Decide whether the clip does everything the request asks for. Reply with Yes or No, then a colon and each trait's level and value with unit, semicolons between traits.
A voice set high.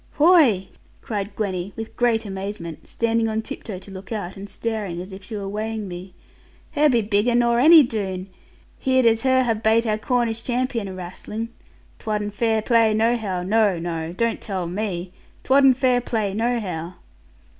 Yes: high, 220 Hz